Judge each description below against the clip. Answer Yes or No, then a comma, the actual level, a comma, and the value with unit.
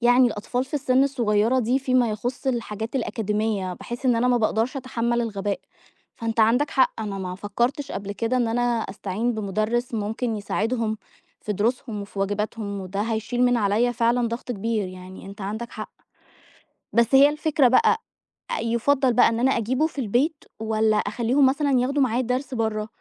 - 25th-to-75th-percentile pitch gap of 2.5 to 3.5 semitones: Yes, average, 3.1 semitones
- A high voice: Yes, high, 230 Hz